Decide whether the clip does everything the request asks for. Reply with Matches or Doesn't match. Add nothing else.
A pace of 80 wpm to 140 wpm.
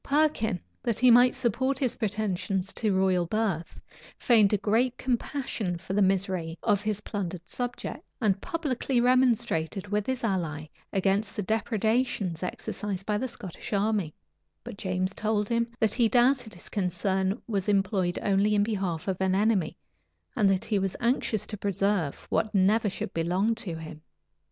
Doesn't match